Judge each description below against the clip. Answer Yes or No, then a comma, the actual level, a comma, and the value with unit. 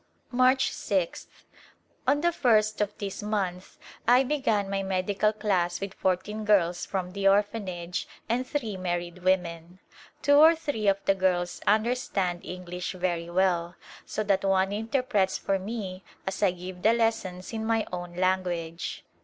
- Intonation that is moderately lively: Yes, average, 3.2 semitones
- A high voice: Yes, high, 195 Hz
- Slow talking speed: No, average, 165 wpm